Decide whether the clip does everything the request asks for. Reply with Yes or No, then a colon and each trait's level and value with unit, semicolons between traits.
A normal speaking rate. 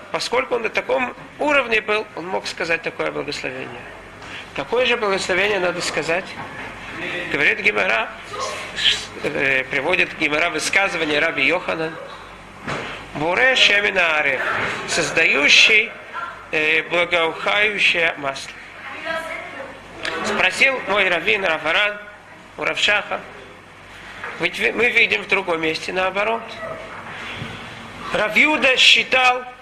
No: slow, 90 wpm